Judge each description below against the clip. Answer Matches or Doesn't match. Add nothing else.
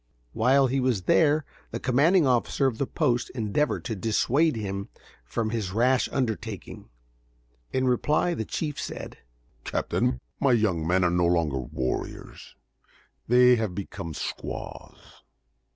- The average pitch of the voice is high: Doesn't match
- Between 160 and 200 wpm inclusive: Doesn't match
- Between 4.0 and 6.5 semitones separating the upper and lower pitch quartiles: Matches